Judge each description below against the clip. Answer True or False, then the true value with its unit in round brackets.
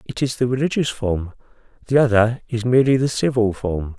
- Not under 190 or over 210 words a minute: False (180 wpm)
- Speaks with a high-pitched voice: False (120 Hz)